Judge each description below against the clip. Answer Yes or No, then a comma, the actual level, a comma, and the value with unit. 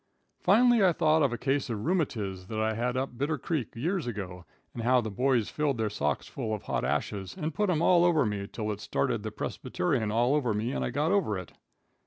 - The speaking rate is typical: No, fast, 235 wpm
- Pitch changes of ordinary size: No, wide, 6.4 semitones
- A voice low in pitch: Yes, low, 125 Hz